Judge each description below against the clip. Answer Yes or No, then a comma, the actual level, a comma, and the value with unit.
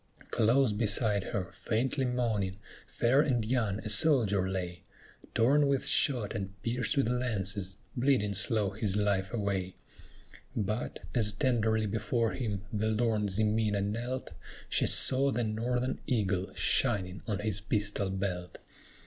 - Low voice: Yes, low, 110 Hz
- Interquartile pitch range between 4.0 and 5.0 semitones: No, average, 3.4 semitones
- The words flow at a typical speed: No, slow, 130 wpm